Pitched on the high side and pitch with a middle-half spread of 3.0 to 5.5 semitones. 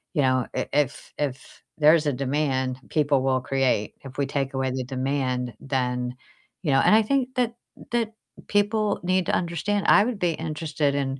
No: medium, 140 Hz; average, 5.0 semitones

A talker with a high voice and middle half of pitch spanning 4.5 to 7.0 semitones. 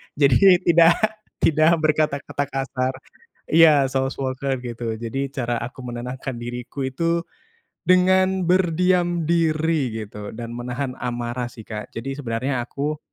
No: low, 135 Hz; average, 5.0 semitones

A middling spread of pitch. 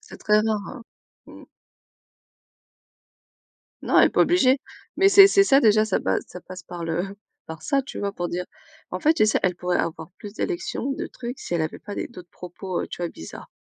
No: wide, 7.7 semitones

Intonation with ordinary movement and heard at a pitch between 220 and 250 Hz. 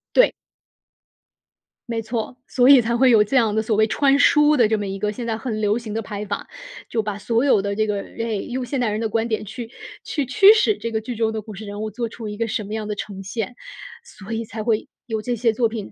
No: narrow, 2.2 semitones; high, 225 Hz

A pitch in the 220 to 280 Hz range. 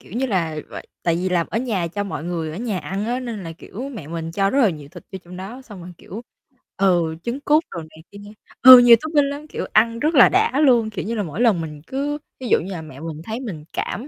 No: high, 200 Hz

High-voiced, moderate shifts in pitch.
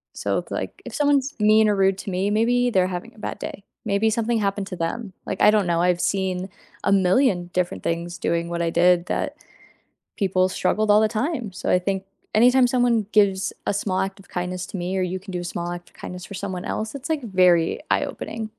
Yes: high, 195 Hz; average, 3.3 semitones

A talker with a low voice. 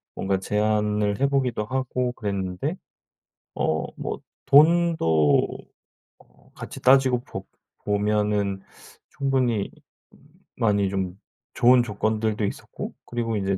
Yes: low, 105 Hz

